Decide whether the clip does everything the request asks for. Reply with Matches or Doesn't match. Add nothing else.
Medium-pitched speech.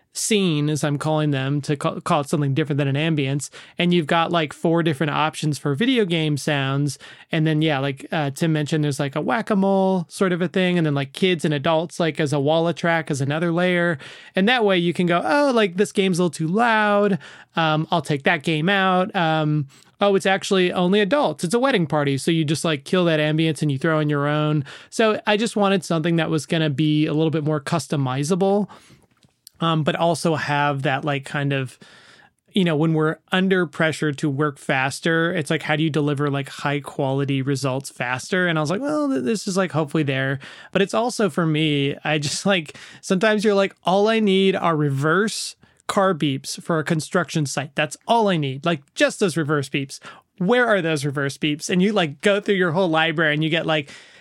Matches